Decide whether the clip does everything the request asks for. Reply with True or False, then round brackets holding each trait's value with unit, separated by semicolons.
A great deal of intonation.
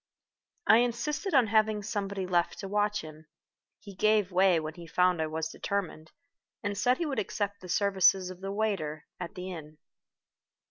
False (3.4 semitones)